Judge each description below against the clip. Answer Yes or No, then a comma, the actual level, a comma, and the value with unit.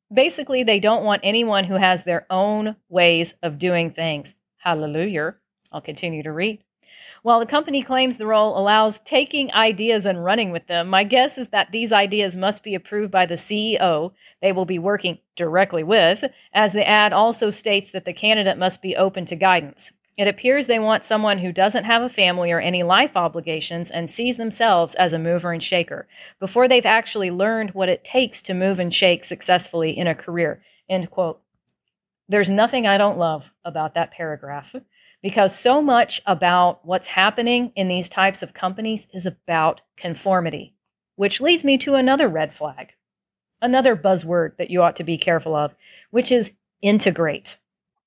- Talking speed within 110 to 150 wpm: No, average, 175 wpm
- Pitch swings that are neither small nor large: Yes, average, 4.0 semitones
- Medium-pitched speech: No, high, 195 Hz